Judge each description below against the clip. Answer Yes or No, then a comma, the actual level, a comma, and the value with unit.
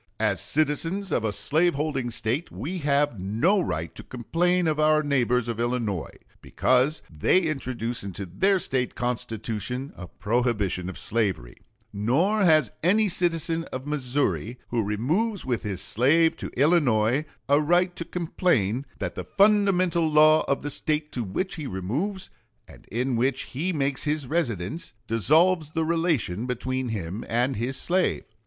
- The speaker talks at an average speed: Yes, average, 150 wpm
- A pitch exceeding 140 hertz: No, low, 135 Hz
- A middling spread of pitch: No, wide, 6.3 semitones